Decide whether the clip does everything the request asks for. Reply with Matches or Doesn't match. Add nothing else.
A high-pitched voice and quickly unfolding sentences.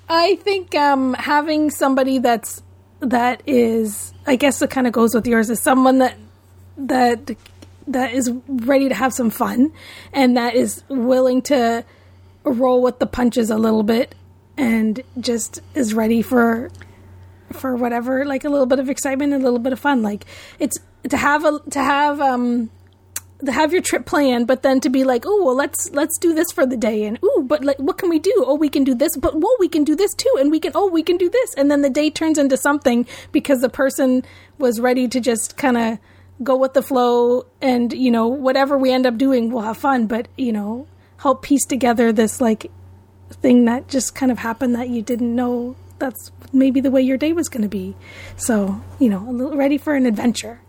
Matches